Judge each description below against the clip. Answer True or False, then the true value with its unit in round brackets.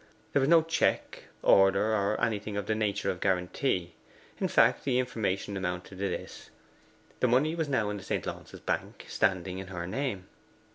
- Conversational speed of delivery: True (180 wpm)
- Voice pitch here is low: True (100 Hz)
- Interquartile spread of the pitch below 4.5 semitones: False (4.8 semitones)